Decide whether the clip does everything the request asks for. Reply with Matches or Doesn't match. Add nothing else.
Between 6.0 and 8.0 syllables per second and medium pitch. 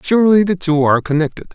Matches